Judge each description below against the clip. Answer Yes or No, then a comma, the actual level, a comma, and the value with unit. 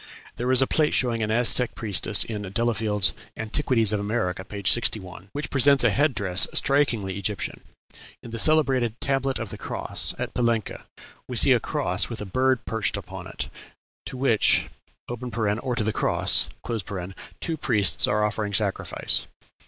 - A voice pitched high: No, low, 115 Hz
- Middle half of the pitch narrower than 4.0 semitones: Yes, average, 3.6 semitones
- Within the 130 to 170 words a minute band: Yes, average, 160 wpm